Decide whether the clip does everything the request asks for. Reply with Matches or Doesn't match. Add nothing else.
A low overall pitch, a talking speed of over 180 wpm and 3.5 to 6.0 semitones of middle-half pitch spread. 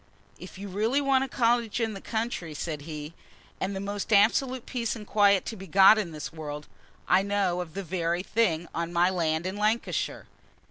Doesn't match